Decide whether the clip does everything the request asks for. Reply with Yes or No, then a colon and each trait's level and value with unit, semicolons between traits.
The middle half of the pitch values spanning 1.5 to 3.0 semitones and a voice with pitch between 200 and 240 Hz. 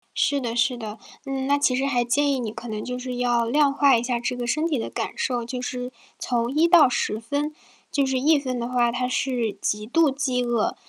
No: narrow, 2.6 semitones; very high, 250 Hz